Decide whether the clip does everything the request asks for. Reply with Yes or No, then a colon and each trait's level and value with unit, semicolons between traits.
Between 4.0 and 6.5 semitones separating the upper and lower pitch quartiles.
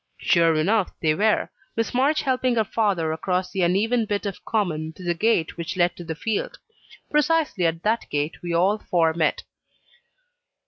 Yes: average, 5.0 semitones